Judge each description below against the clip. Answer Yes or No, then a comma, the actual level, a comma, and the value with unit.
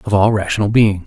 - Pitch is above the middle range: No, low, 105 Hz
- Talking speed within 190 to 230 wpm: Yes, fast, 225 wpm